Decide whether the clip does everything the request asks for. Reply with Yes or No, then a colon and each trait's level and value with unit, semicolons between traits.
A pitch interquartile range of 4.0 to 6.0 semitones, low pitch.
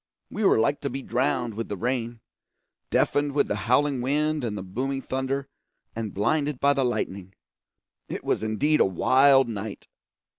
Yes: average, 4.3 semitones; low, 130 Hz